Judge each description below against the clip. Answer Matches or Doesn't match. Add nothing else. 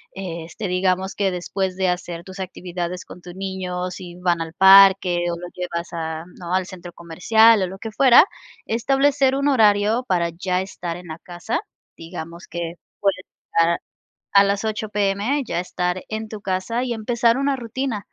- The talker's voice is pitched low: Doesn't match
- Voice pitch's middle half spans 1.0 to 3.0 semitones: Doesn't match